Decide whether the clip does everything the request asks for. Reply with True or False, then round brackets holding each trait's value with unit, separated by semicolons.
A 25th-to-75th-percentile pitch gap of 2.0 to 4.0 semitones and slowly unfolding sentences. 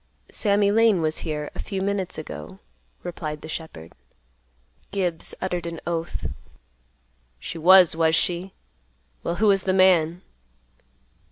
True (3.1 semitones; 125 wpm)